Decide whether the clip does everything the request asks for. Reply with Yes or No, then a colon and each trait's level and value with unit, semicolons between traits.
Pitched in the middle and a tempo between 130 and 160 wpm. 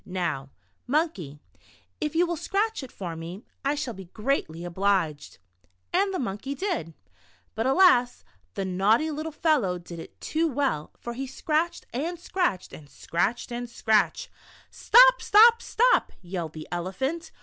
No: high, 245 Hz; average, 150 wpm